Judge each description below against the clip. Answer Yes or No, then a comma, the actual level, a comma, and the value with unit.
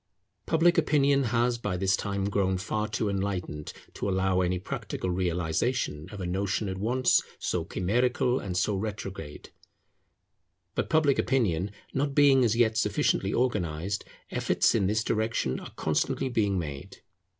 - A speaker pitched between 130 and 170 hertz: No, low, 100 Hz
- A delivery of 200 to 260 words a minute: No, average, 145 wpm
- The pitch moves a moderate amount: Yes, average, 4.9 semitones